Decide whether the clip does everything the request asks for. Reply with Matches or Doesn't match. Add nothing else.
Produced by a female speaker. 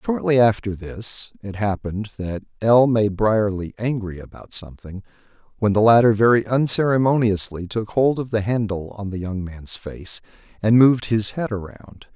Doesn't match